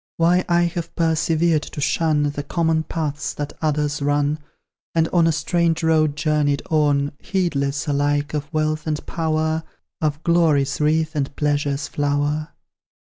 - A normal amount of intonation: No, narrow, 1.9 semitones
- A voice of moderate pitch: Yes, medium, 155 Hz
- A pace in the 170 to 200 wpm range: No, average, 145 wpm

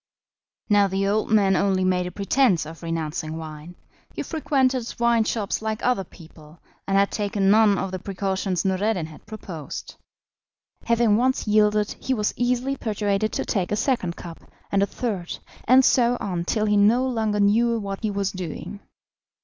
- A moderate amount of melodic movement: Yes, average, 3.4 semitones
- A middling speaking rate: Yes, average, 170 wpm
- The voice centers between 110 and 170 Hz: No, high, 205 Hz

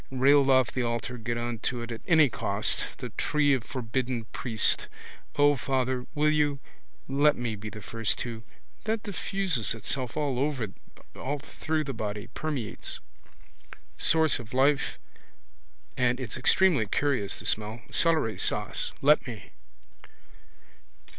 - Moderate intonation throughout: Yes, average, 4.0 semitones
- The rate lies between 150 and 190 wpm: No, slow, 135 wpm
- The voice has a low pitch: Yes, low, 130 Hz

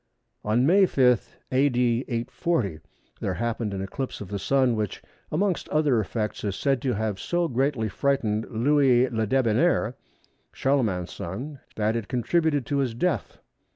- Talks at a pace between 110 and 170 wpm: Yes, average, 150 wpm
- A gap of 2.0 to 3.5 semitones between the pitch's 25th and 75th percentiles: No, average, 4.4 semitones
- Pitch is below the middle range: Yes, low, 125 Hz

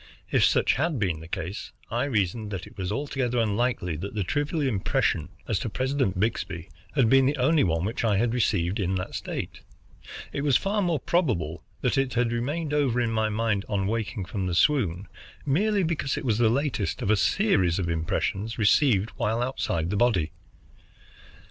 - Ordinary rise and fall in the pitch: No, wide, 5.9 semitones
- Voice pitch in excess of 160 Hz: No, low, 115 Hz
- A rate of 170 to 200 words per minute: Yes, average, 185 wpm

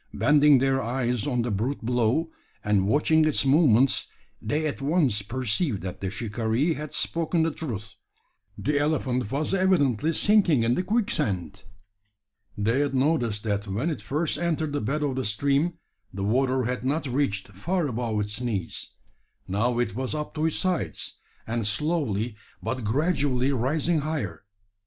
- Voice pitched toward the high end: No, low, 130 Hz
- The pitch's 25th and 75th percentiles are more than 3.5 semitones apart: Yes, wide, 5.5 semitones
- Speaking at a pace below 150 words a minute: No, average, 155 wpm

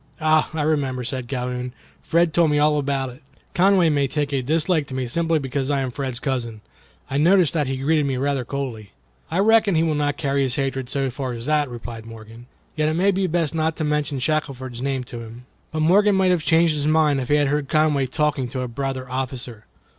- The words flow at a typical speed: No, fast, 225 wpm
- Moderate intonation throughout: Yes, average, 3.4 semitones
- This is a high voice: No, medium, 140 Hz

